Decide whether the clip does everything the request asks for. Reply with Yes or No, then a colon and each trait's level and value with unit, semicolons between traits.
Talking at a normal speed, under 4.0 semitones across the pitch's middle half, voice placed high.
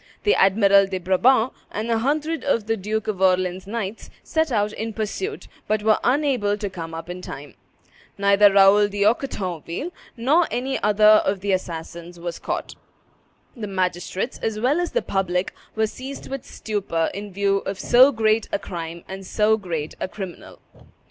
Yes: average, 170 wpm; average, 3.3 semitones; high, 205 Hz